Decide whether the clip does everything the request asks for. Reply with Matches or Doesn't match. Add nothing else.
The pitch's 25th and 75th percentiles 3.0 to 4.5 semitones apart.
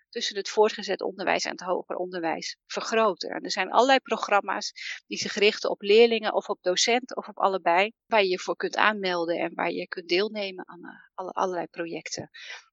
Matches